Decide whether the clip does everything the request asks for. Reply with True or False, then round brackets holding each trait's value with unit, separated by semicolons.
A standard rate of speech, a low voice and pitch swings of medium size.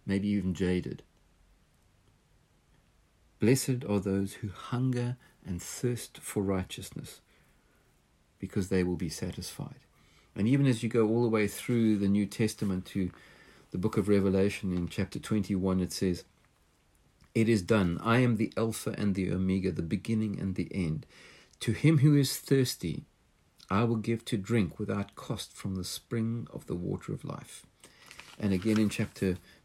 True (160 wpm; 100 Hz; 3.6 semitones)